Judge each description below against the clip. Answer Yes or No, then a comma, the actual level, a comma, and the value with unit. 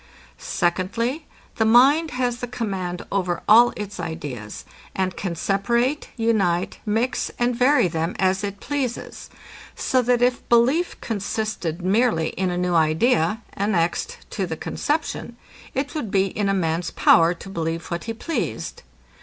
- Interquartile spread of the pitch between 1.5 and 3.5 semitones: No, wide, 5.5 semitones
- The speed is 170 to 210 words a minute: No, average, 145 wpm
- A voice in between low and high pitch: No, high, 205 Hz